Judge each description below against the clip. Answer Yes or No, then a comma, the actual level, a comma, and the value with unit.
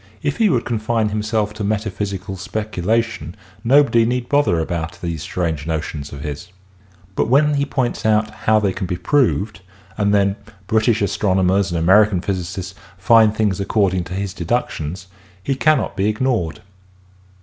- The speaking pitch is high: No, low, 105 Hz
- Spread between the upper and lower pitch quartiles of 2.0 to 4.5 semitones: Yes, average, 3.8 semitones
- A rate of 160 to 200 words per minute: No, average, 150 wpm